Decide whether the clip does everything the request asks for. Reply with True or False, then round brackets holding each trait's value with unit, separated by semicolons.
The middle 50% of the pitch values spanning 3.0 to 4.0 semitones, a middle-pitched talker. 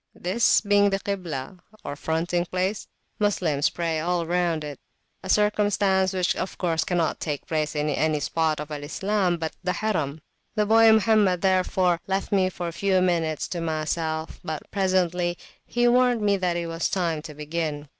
True (3.5 semitones; 175 Hz)